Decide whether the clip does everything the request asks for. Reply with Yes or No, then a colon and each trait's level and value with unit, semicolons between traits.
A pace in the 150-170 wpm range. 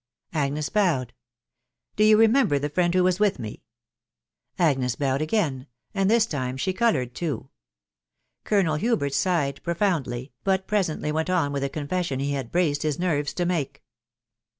Yes: average, 165 wpm